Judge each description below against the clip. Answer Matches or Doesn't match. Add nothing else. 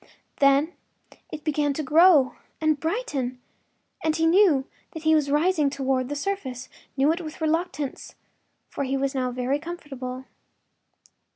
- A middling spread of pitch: Matches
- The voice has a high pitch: Matches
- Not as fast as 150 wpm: Matches